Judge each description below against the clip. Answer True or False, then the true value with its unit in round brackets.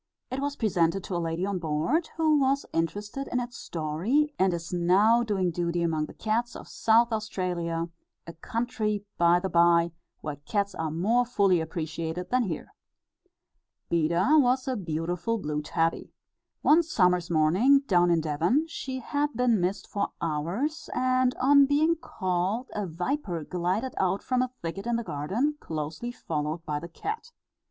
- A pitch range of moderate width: False (6.8 semitones)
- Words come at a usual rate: True (160 wpm)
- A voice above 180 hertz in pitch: True (190 Hz)